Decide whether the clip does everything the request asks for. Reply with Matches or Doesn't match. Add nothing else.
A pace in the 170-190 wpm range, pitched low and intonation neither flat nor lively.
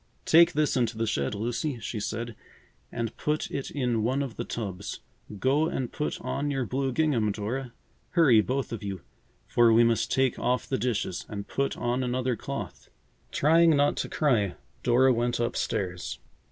Matches